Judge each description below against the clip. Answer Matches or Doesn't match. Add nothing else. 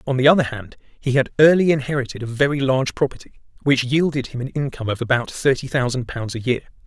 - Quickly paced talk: Matches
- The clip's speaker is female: Doesn't match